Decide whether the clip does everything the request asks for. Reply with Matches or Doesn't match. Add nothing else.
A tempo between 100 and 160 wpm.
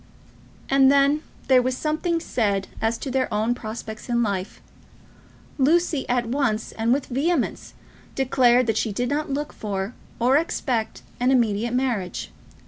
Matches